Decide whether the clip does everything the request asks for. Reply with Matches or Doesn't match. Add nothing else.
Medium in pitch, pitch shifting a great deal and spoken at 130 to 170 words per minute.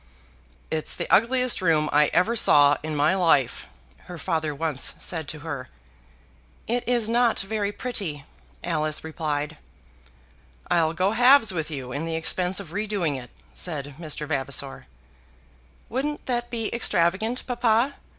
Matches